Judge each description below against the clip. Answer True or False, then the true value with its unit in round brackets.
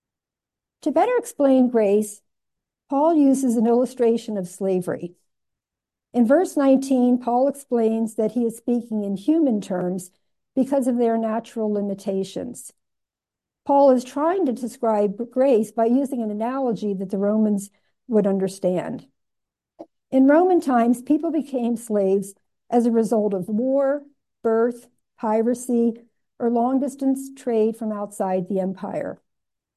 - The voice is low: False (235 Hz)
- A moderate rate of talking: False (125 wpm)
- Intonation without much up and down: False (4.2 semitones)